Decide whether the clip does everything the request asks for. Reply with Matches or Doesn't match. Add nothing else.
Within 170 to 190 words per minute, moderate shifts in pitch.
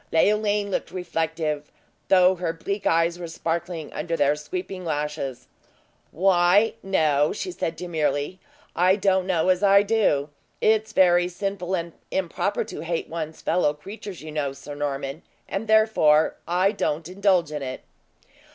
Doesn't match